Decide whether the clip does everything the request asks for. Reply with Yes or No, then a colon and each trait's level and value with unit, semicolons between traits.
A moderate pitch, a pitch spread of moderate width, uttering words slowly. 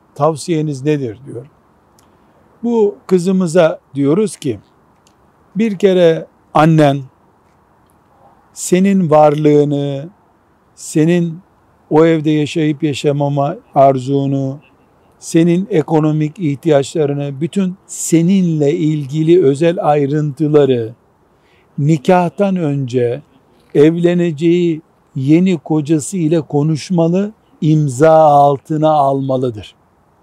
Yes: medium, 155 Hz; average, 3.2 semitones; slow, 70 wpm